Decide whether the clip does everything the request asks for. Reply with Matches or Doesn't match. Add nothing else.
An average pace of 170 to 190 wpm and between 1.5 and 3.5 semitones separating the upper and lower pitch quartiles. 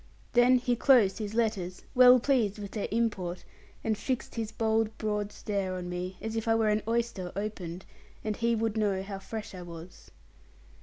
Matches